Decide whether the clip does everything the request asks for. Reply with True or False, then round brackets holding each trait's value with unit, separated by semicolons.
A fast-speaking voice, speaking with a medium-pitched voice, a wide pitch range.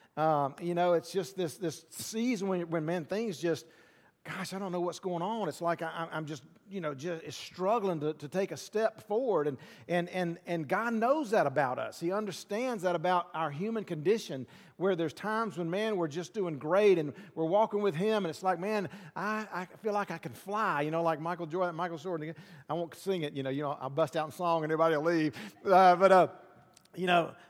False (225 wpm; 175 Hz; 3.2 semitones)